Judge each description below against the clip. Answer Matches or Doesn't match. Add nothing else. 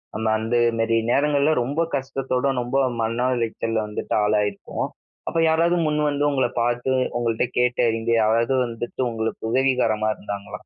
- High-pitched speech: Doesn't match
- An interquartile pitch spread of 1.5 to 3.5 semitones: Matches